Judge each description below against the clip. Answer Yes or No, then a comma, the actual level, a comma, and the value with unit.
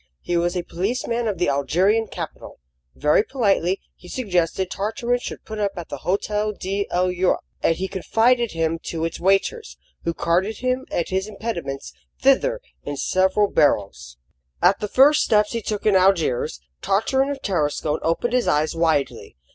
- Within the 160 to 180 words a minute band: Yes, average, 165 wpm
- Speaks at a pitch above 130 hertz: Yes, high, 190 Hz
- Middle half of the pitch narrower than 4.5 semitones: No, average, 5.0 semitones